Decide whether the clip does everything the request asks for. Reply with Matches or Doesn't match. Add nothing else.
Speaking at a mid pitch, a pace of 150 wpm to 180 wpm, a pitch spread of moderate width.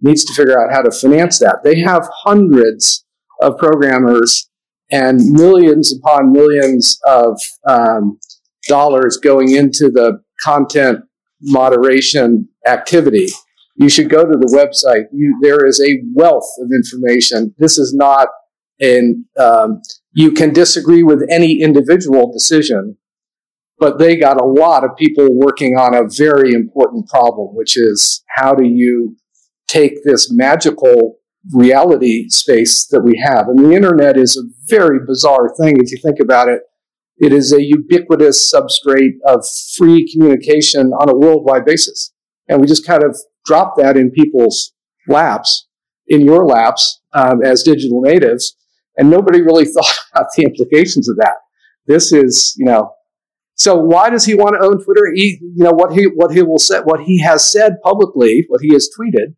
Matches